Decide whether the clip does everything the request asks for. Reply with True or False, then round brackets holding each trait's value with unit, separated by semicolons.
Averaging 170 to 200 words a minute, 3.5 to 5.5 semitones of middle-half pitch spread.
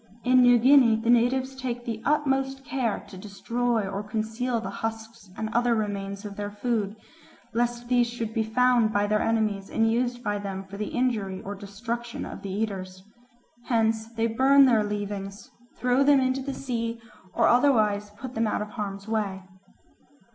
False (175 wpm; 3.0 semitones)